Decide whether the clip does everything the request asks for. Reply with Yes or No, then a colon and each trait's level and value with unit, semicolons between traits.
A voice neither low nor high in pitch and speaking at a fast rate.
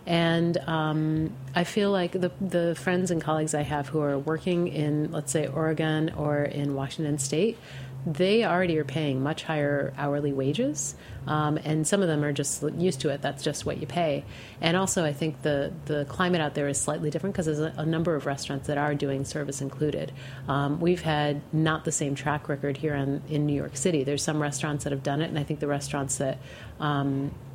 Yes: medium, 150 Hz; fast, 215 wpm